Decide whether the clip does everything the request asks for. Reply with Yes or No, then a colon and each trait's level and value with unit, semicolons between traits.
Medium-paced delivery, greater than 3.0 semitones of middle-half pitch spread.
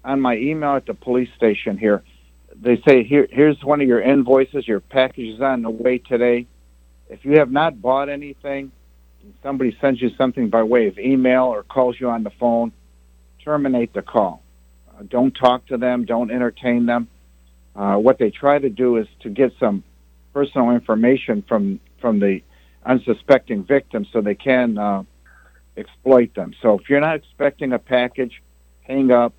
No: fast, 180 wpm; average, 4.7 semitones